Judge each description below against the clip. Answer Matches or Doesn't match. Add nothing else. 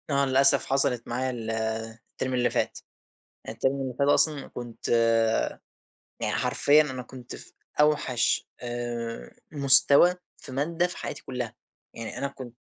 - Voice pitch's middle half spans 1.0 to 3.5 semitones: Matches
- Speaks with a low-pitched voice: Matches